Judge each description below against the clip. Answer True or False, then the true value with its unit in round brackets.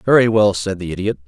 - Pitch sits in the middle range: False (100 Hz)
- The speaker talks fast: True (235 wpm)